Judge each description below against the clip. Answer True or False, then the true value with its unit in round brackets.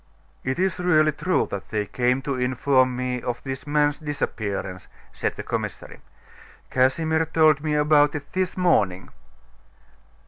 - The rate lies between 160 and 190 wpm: False (140 wpm)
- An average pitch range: True (3.7 semitones)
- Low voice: False (145 Hz)